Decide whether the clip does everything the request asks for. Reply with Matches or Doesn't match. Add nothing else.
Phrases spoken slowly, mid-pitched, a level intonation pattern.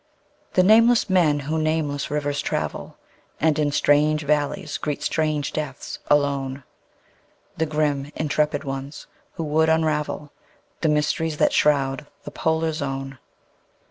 Matches